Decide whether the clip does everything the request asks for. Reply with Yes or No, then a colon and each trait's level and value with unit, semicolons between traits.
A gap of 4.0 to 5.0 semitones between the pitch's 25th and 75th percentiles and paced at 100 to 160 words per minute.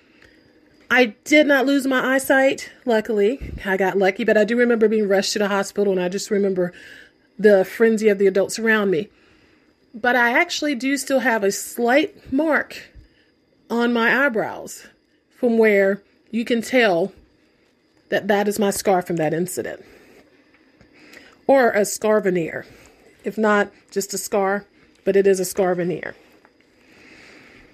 Yes: average, 4.4 semitones; average, 150 wpm